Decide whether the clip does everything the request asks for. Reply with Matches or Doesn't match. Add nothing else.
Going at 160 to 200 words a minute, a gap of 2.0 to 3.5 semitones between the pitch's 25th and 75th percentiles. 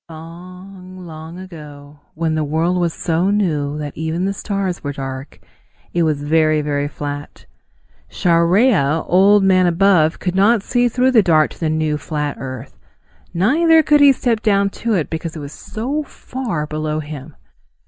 Doesn't match